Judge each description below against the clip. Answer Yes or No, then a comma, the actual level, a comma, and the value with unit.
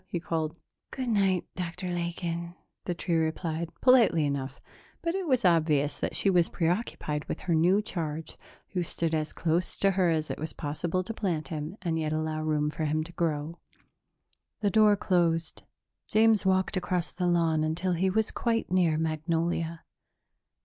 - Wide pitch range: No, average, 2.9 semitones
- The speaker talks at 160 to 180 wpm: Yes, average, 170 wpm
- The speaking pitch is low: No, medium, 170 Hz